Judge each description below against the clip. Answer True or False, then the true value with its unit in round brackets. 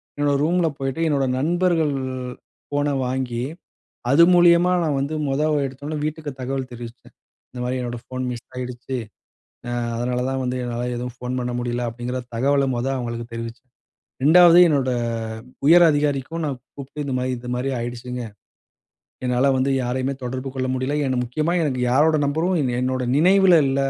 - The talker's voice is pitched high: False (130 Hz)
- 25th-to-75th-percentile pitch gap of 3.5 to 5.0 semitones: False (3.1 semitones)